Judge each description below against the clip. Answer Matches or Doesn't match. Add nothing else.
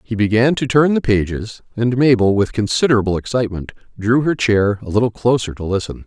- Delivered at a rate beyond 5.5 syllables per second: Matches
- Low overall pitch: Matches